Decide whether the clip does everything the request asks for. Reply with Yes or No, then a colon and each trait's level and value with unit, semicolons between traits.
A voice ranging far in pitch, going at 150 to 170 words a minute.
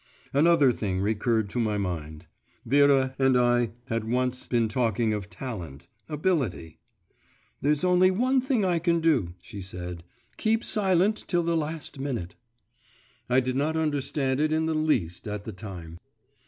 Yes: wide, 7.3 semitones; average, 155 wpm